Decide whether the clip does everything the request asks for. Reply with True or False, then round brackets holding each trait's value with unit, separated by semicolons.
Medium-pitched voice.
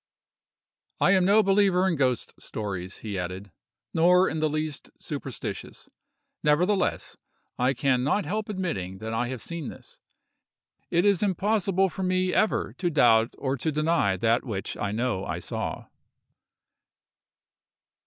True (155 Hz)